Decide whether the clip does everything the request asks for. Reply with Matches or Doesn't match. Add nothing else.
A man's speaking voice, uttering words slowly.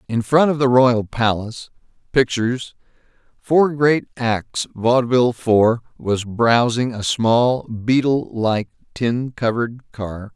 Matches